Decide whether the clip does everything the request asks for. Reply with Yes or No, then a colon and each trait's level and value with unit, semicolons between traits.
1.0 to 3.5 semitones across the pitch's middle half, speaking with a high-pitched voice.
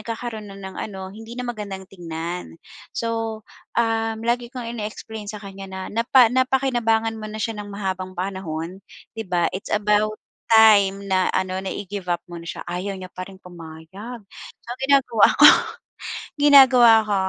Yes: average, 3.2 semitones; high, 210 Hz